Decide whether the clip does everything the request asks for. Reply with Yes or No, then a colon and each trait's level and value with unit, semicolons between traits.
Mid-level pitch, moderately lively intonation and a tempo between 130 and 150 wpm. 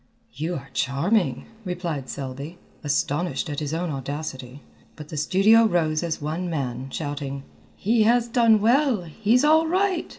No: medium, 165 Hz; wide, 7.4 semitones; average, 145 wpm